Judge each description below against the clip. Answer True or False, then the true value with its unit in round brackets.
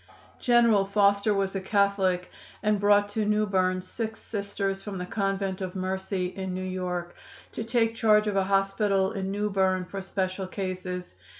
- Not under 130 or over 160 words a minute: False (170 wpm)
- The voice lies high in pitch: True (195 Hz)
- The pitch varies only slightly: True (1.6 semitones)